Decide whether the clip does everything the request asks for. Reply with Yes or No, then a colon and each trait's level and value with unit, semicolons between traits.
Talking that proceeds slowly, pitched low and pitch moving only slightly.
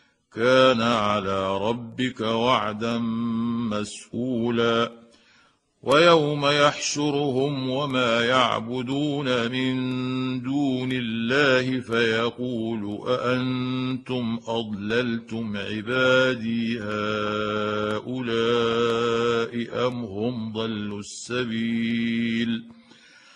Yes: slow, 55 wpm; low, 120 Hz; narrow, 2.1 semitones